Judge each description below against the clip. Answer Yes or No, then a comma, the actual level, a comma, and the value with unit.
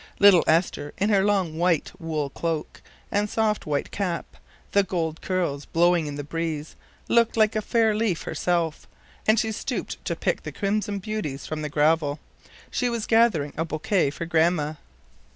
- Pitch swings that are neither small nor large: Yes, average, 4.9 semitones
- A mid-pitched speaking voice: Yes, medium, 175 Hz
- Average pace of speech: Yes, average, 170 wpm